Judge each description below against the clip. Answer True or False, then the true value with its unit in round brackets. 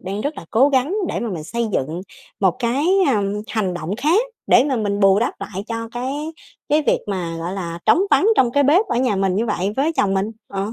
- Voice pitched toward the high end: True (220 Hz)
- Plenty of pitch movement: True (5.9 semitones)